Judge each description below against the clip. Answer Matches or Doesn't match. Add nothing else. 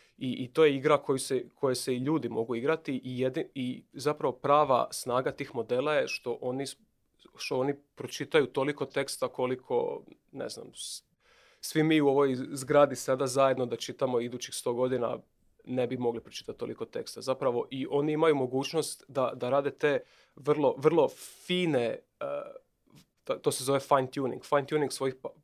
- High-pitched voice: Doesn't match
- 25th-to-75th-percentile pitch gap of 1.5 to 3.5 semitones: Matches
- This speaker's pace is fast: Matches